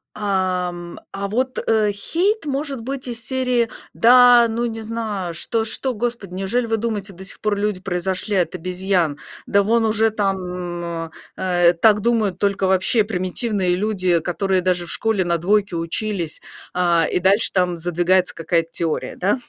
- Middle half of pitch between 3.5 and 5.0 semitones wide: Yes, average, 3.9 semitones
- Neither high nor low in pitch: No, high, 195 Hz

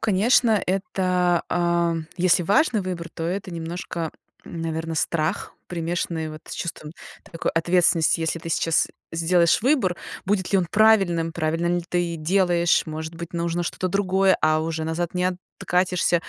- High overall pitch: No, medium, 175 Hz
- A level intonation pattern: Yes, narrow, 2.0 semitones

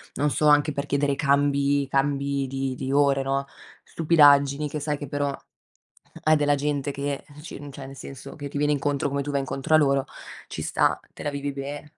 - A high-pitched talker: No, medium, 140 Hz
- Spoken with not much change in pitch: Yes, narrow, 1.0 semitones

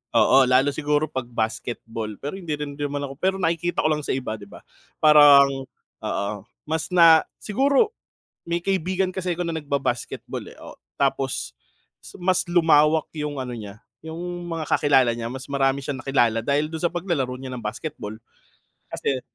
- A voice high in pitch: No, medium, 145 Hz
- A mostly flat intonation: No, average, 4.6 semitones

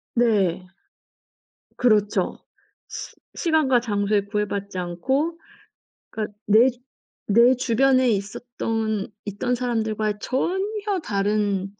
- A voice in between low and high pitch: No, high, 220 Hz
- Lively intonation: No, average, 3.9 semitones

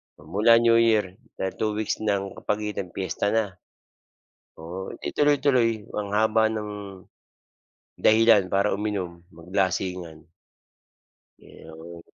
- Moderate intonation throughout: Yes, average, 3.1 semitones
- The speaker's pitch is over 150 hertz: No, low, 105 Hz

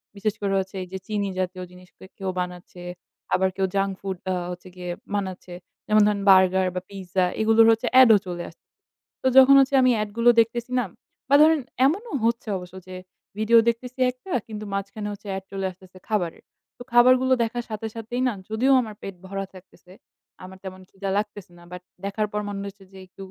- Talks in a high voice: Yes, high, 200 Hz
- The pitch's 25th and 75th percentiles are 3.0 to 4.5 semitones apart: Yes, average, 3.5 semitones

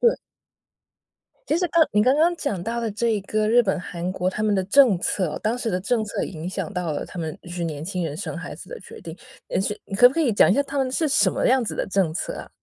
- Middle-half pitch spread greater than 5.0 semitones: Yes, wide, 5.4 semitones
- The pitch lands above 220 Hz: No, high, 210 Hz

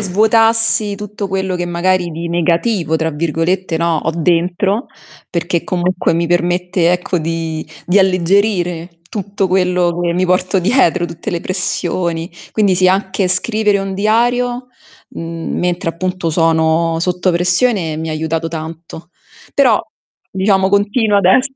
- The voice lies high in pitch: No, medium, 180 Hz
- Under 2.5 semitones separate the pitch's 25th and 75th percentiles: No, average, 2.8 semitones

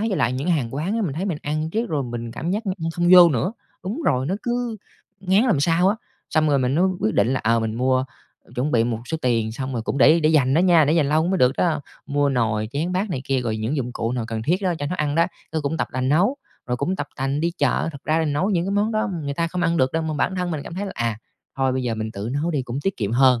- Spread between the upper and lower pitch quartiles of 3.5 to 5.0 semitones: No, wide, 5.6 semitones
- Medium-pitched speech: Yes, medium, 150 Hz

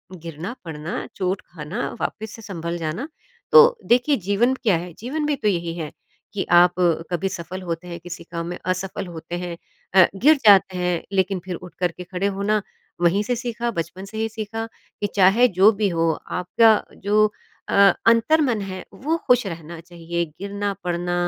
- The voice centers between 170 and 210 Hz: Yes, high, 190 Hz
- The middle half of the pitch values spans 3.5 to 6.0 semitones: Yes, average, 4.0 semitones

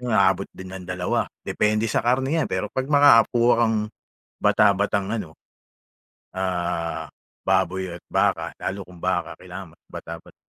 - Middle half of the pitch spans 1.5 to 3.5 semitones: No, average, 4.1 semitones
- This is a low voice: Yes, very low, 95 Hz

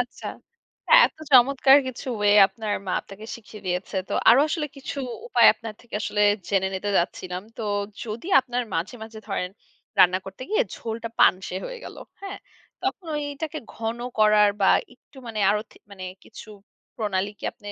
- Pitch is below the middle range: No, high, 220 Hz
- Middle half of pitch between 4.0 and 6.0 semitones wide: Yes, average, 4.5 semitones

